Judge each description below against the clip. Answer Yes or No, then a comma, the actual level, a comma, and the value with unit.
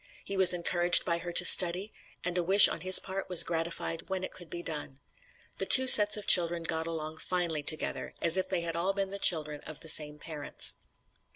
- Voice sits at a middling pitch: Yes, medium, 170 Hz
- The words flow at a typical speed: No, fast, 215 wpm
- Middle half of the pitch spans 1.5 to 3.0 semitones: Yes, narrow, 2.5 semitones